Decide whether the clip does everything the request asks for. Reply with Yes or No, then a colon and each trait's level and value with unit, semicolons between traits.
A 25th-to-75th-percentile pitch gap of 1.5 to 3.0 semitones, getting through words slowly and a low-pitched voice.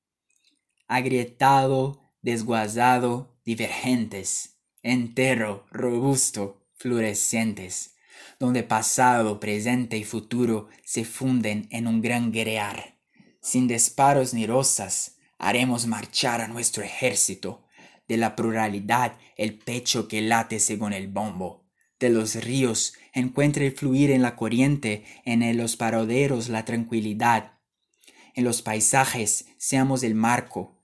Yes: narrow, 2.4 semitones; slow, 110 wpm; low, 115 Hz